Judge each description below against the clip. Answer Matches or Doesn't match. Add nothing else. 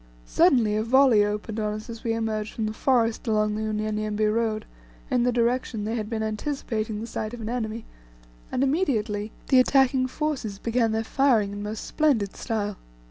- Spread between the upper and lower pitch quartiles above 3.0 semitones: Doesn't match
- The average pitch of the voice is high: Matches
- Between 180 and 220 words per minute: Matches